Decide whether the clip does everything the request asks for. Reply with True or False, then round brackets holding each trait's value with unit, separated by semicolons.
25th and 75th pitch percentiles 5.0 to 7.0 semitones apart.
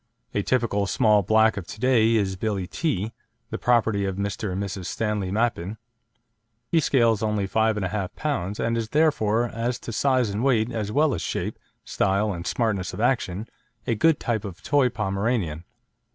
False (3.2 semitones)